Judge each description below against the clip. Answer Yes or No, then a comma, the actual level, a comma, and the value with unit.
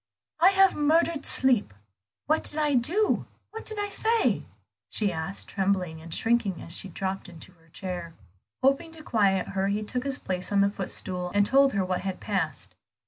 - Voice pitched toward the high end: Yes, high, 200 Hz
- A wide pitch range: Yes, wide, 8.0 semitones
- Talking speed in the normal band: Yes, average, 185 wpm